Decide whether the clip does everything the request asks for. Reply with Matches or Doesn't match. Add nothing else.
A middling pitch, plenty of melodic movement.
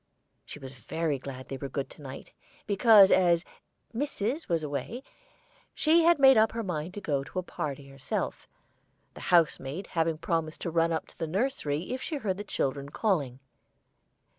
Matches